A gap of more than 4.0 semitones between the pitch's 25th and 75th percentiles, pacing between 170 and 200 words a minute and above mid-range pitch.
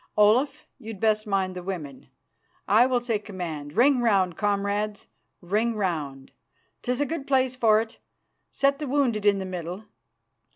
No: average, 4.8 semitones; average, 155 wpm; high, 210 Hz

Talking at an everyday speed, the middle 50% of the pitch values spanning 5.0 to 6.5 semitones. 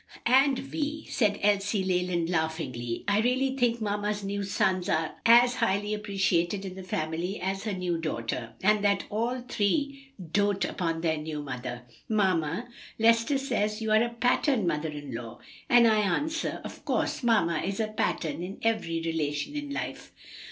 Yes: average, 165 wpm; wide, 5.6 semitones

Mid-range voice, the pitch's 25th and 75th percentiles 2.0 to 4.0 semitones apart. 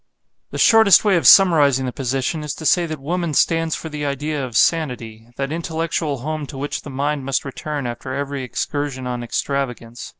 Yes: medium, 145 Hz; average, 3.3 semitones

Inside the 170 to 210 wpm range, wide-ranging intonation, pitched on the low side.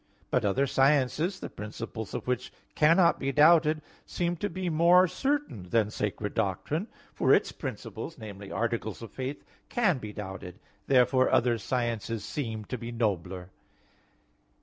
No: average, 145 wpm; wide, 6.4 semitones; low, 125 Hz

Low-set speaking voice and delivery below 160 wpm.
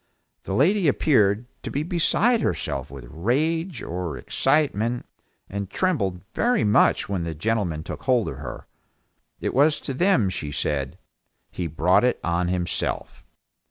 Yes: low, 105 Hz; average, 145 wpm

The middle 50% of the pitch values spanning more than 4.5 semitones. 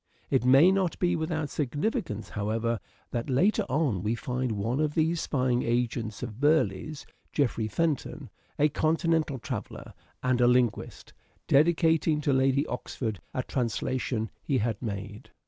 Yes: average, 5.1 semitones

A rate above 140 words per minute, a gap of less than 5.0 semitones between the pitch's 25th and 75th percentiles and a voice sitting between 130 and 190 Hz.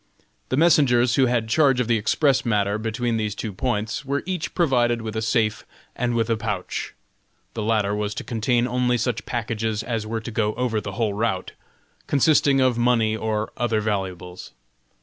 No: average, 180 wpm; narrow, 2.5 semitones; low, 115 Hz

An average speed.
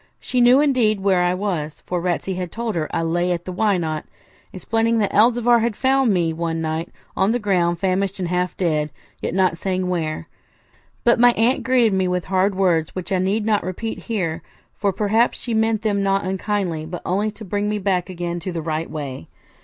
No: fast, 210 wpm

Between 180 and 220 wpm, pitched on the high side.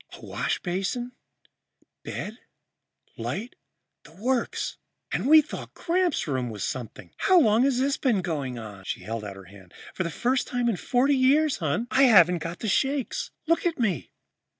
No: average, 165 wpm; high, 220 Hz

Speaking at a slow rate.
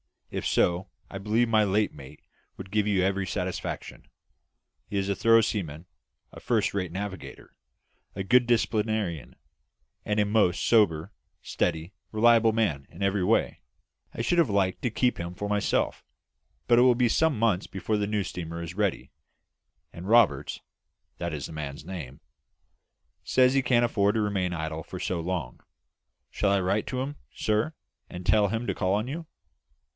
No: average, 170 wpm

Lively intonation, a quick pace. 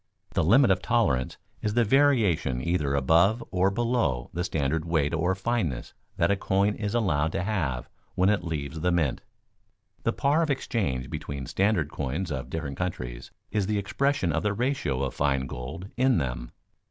No: wide, 7.0 semitones; average, 175 wpm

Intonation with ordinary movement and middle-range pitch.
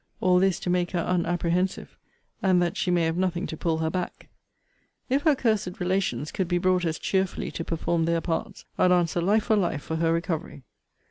No: narrow, 1.9 semitones; medium, 175 Hz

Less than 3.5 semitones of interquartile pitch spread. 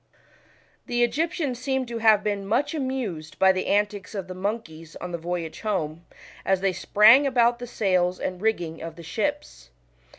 No: average, 5.2 semitones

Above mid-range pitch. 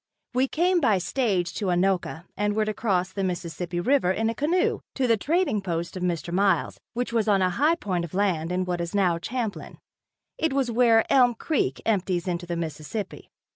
Yes: high, 195 Hz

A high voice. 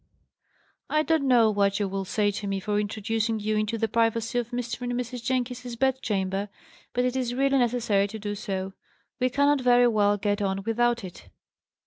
Yes: high, 225 Hz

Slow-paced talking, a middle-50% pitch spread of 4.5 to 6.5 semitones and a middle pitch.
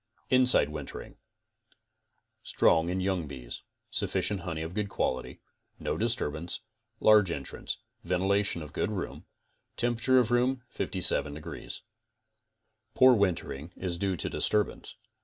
No: slow, 120 wpm; average, 5.1 semitones; very low, 95 Hz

